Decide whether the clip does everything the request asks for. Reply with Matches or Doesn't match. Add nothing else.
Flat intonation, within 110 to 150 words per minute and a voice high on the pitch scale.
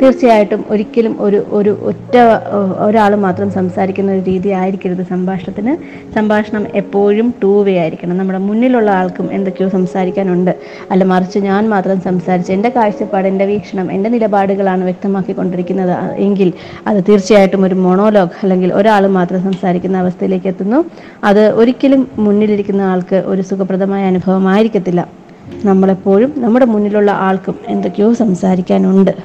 Matches